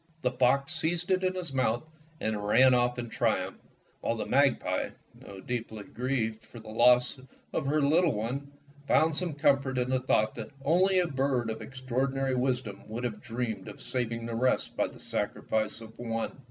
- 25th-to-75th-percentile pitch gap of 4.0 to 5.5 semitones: No, average, 3.4 semitones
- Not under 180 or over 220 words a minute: Yes, average, 185 wpm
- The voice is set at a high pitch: No, low, 125 Hz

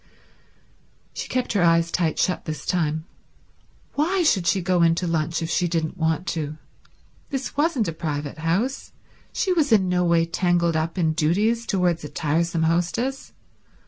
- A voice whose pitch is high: No, medium, 170 Hz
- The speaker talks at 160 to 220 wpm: Yes, average, 165 wpm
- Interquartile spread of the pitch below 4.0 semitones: Yes, average, 3.5 semitones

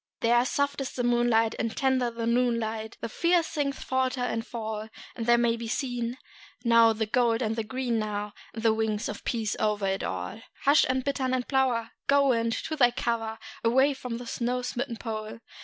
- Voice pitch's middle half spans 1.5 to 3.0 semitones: Yes, narrow, 2.4 semitones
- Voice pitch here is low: No, high, 235 Hz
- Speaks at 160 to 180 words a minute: No, average, 195 wpm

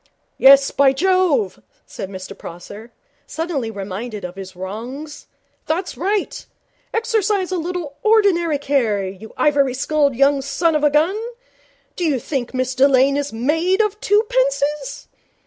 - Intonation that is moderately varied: No, wide, 6.8 semitones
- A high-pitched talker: Yes, very high, 285 Hz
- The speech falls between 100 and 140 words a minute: Yes, slow, 135 wpm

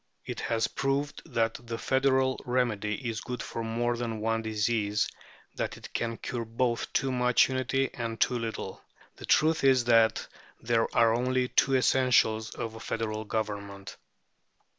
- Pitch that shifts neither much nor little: No, narrow, 2.2 semitones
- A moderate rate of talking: Yes, average, 155 wpm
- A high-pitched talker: No, low, 115 Hz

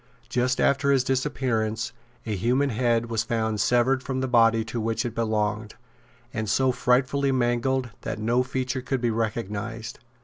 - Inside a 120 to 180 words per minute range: Yes, average, 160 wpm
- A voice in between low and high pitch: No, low, 120 Hz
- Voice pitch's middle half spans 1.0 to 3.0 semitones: Yes, narrow, 2.5 semitones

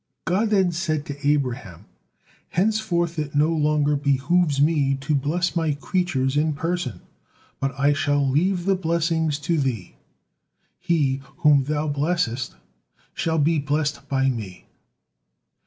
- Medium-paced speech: No, slow, 130 wpm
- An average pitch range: Yes, average, 3.4 semitones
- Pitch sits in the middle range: Yes, medium, 150 Hz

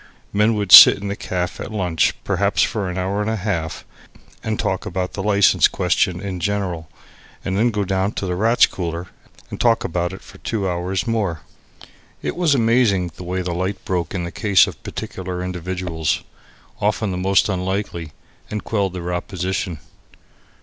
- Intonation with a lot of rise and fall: No, narrow, 2.5 semitones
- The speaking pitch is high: No, very low, 95 Hz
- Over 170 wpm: Yes, average, 180 wpm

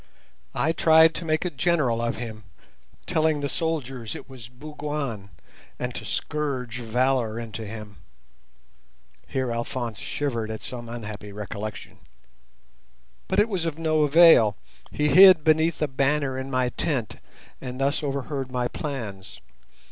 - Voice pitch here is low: Yes, low, 130 Hz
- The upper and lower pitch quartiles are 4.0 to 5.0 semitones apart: Yes, average, 4.6 semitones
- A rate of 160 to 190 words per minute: No, average, 140 wpm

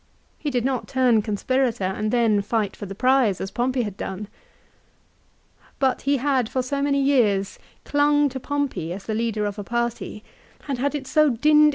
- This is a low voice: No, high, 245 Hz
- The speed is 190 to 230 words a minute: Yes, average, 200 wpm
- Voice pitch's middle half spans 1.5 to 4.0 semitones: No, average, 4.7 semitones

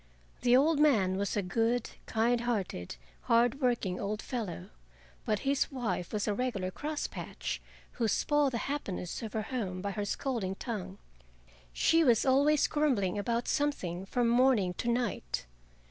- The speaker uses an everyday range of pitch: Yes, average, 4.9 semitones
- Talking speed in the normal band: Yes, average, 155 wpm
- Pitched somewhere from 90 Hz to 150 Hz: No, high, 230 Hz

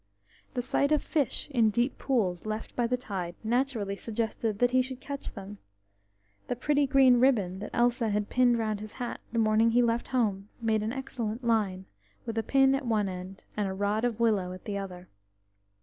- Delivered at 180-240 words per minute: Yes, average, 200 wpm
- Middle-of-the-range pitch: No, high, 225 Hz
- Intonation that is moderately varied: Yes, average, 3.4 semitones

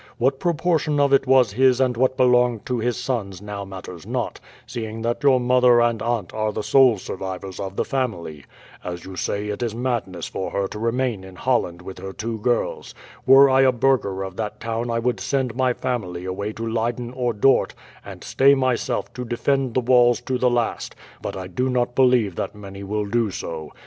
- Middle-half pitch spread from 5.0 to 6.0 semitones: No, average, 4.1 semitones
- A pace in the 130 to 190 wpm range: No, fast, 205 wpm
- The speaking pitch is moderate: No, low, 120 Hz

